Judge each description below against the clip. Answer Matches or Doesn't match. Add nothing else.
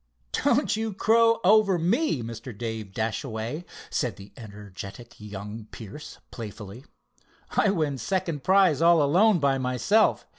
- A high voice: Doesn't match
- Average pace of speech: Doesn't match